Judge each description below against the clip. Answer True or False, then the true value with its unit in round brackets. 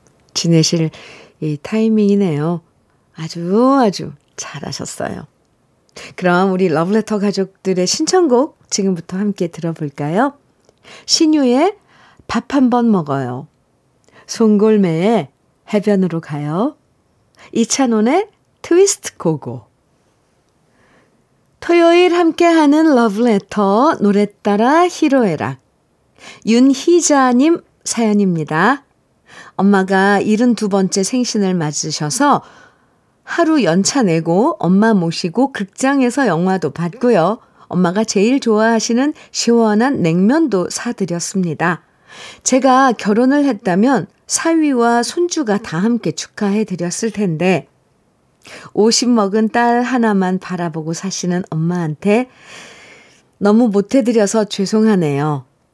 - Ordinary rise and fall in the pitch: False (6.1 semitones)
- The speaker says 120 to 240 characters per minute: True (230 characters per minute)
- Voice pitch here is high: True (210 Hz)